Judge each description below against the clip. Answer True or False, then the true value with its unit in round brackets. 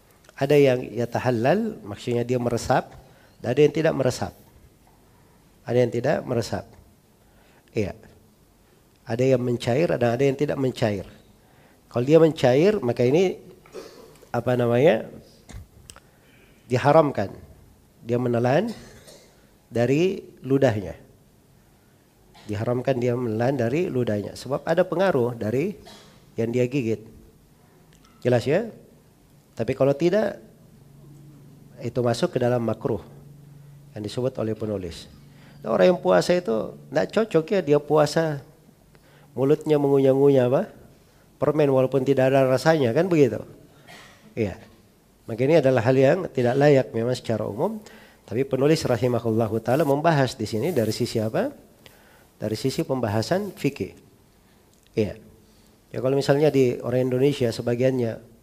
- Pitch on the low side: True (125 Hz)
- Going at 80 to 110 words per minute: False (120 wpm)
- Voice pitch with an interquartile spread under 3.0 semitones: False (4.0 semitones)